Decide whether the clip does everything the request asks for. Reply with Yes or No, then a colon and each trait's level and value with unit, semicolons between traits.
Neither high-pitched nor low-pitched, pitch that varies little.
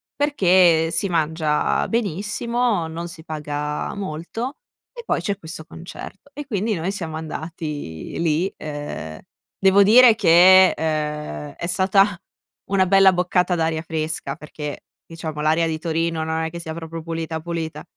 No: medium, 165 Hz; average, 3.2 semitones